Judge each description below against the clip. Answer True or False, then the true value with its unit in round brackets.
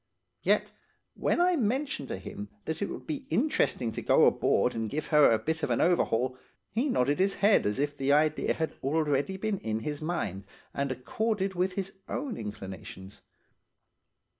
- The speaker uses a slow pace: False (175 wpm)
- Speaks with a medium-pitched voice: True (155 Hz)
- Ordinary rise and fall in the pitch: False (7.9 semitones)